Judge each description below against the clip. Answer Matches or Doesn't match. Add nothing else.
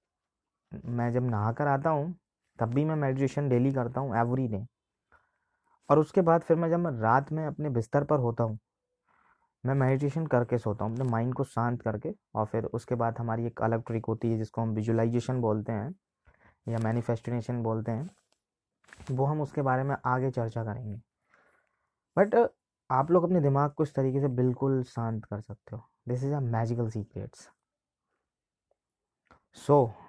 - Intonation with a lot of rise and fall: Doesn't match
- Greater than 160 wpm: Matches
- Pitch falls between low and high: Doesn't match